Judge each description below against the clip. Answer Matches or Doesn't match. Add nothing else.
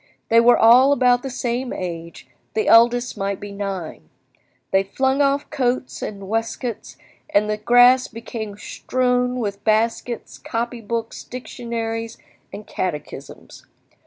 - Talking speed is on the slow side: Matches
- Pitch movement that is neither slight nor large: Matches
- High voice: Matches